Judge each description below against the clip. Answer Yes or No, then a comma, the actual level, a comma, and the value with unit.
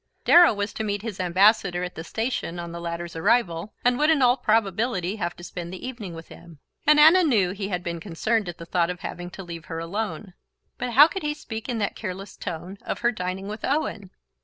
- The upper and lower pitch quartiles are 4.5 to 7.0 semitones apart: Yes, average, 4.9 semitones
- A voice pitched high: Yes, high, 195 Hz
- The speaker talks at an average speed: No, fast, 230 wpm